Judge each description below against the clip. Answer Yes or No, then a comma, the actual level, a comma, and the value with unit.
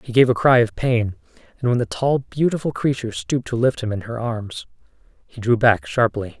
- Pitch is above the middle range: No, low, 115 Hz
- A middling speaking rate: No, fast, 215 wpm